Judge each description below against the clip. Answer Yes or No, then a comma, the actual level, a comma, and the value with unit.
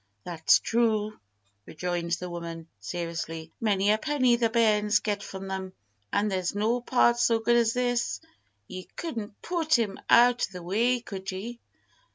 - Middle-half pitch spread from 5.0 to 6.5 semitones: No, average, 4.4 semitones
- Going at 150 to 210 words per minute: Yes, average, 160 wpm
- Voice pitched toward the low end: No, high, 210 Hz